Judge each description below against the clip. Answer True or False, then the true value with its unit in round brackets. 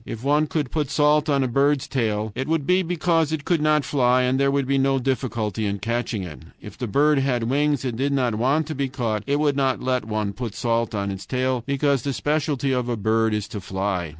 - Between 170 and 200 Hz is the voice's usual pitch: False (130 Hz)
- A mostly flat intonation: False (4.1 semitones)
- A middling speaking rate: False (240 wpm)